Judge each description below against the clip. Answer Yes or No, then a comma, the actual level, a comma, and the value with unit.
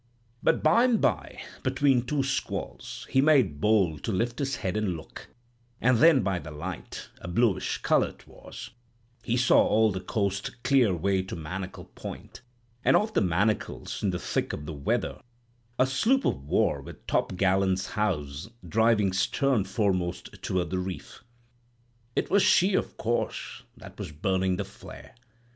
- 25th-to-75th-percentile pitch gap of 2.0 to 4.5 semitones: No, average, 5.1 semitones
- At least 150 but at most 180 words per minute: Yes, average, 155 wpm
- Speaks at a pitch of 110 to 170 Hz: No, low, 100 Hz